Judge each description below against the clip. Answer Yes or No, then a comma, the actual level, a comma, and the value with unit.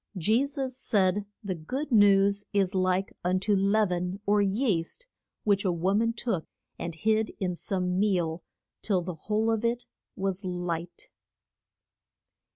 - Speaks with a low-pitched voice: No, high, 195 Hz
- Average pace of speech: Yes, average, 150 wpm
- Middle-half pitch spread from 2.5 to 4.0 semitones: Yes, average, 3.1 semitones